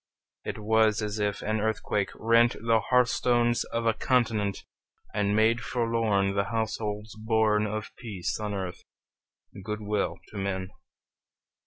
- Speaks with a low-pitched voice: Yes, low, 110 Hz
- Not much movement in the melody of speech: Yes, narrow, 1.8 semitones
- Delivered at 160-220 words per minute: No, average, 140 wpm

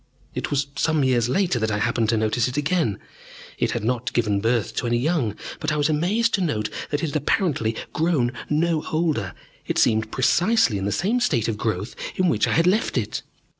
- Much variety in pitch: Yes, wide, 6.7 semitones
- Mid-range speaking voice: No, low, 130 Hz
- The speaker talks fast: Yes, fast, 210 wpm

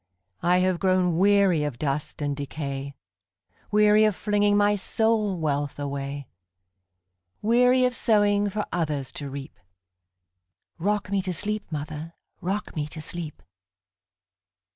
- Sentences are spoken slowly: Yes, slow, 110 wpm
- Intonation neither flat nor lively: No, wide, 7.1 semitones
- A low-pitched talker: No, medium, 155 Hz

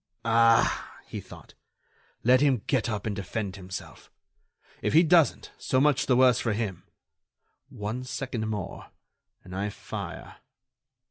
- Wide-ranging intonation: No, average, 3.9 semitones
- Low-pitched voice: Yes, low, 115 Hz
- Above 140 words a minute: No, slow, 135 wpm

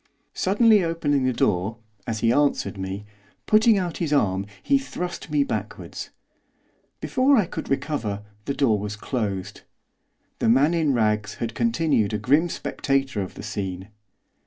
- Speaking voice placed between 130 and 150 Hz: Yes, low, 135 Hz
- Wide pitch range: Yes, wide, 7.9 semitones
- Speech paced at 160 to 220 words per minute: No, average, 150 wpm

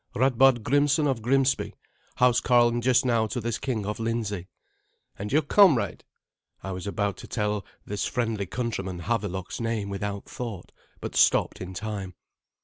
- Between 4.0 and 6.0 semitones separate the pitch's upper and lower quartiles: No, average, 3.6 semitones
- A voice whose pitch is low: Yes, low, 115 Hz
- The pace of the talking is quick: No, average, 145 wpm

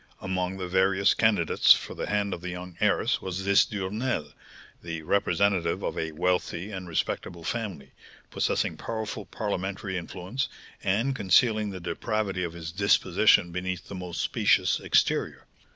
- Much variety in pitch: No, narrow, 2.6 semitones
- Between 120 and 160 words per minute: Yes, average, 145 wpm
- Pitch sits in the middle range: No, very low, 95 Hz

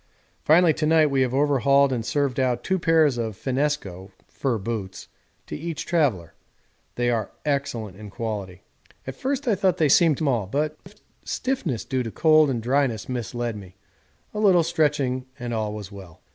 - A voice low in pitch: Yes, low, 130 Hz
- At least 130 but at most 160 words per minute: No, average, 170 wpm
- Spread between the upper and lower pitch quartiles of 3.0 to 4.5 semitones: No, wide, 5.5 semitones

